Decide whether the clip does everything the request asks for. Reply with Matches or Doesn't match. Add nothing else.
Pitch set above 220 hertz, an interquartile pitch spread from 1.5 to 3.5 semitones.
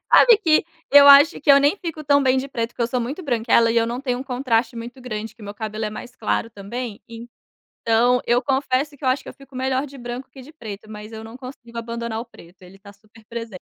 Matches